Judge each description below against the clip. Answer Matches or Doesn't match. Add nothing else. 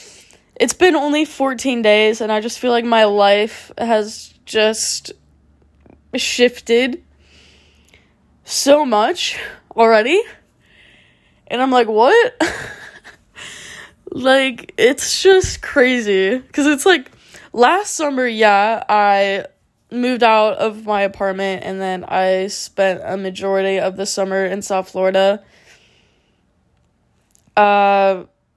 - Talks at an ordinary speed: Doesn't match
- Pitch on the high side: Matches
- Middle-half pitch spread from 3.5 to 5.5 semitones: Matches